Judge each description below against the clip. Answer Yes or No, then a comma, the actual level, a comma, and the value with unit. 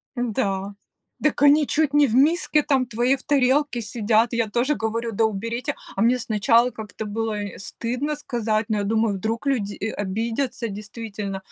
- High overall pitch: Yes, high, 230 Hz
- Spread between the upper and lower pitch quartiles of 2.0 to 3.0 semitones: No, average, 3.5 semitones